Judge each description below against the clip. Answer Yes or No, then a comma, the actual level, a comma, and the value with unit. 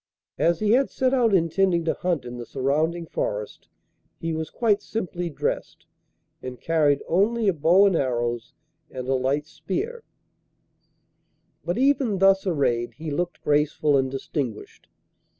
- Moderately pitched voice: Yes, medium, 165 Hz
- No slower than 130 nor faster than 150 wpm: Yes, average, 145 wpm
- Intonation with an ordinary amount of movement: No, wide, 6.0 semitones